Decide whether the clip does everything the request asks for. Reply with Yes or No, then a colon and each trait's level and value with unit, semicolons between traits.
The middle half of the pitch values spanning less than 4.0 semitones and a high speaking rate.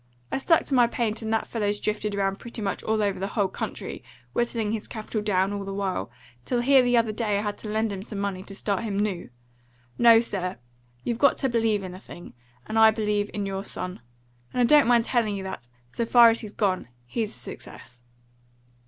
Yes: average, 2.7 semitones; fast, 220 wpm